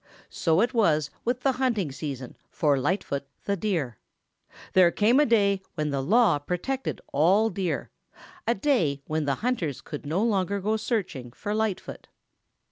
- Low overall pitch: No, high, 190 Hz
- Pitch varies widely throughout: Yes, wide, 6.7 semitones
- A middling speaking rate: Yes, average, 155 wpm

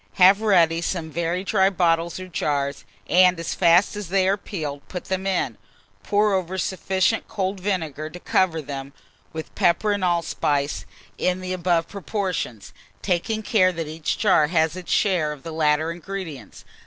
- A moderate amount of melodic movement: Yes, average, 3.1 semitones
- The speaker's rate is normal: Yes, average, 165 wpm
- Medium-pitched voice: Yes, medium, 175 Hz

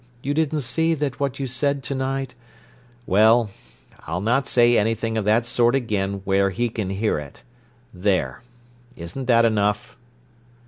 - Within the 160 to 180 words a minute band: No, average, 150 wpm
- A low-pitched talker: Yes, low, 115 Hz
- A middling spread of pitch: Yes, average, 4.6 semitones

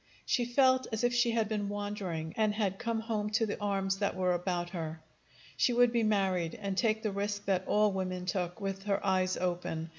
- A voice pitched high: Yes, high, 200 Hz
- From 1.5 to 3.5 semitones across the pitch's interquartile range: Yes, average, 3.0 semitones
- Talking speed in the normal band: No, fast, 210 wpm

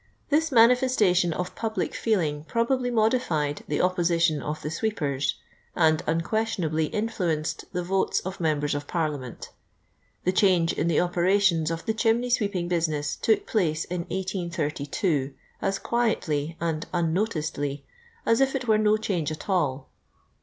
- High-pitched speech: No, medium, 175 Hz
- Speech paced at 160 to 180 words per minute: No, average, 140 wpm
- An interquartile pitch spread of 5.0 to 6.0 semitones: Yes, wide, 5.6 semitones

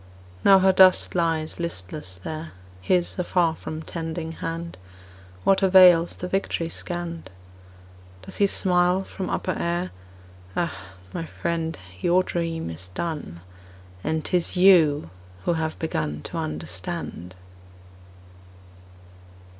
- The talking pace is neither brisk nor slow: No, slow, 115 wpm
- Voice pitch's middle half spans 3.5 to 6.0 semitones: No, narrow, 2.4 semitones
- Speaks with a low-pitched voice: No, medium, 165 Hz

